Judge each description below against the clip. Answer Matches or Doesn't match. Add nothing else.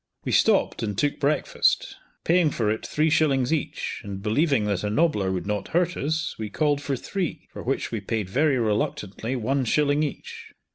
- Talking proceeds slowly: Doesn't match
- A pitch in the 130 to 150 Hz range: Matches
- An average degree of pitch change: Doesn't match